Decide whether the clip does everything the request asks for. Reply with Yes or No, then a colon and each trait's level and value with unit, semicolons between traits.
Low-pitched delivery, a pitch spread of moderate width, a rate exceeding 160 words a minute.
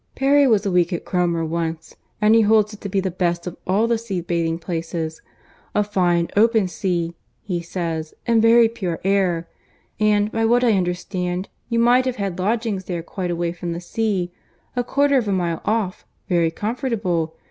No: high, 190 Hz; average, 4.4 semitones; average, 180 wpm